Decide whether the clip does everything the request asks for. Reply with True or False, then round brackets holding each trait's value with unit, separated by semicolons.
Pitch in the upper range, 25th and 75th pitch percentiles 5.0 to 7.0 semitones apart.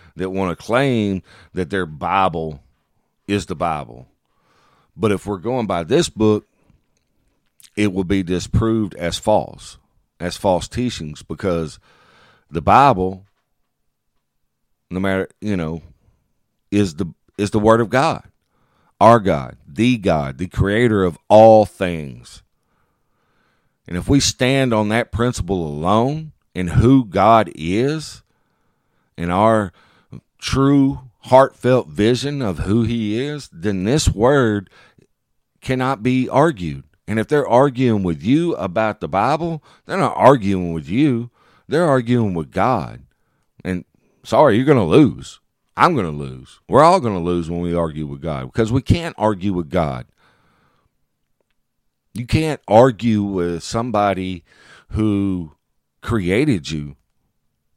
False (100 Hz; 5.3 semitones)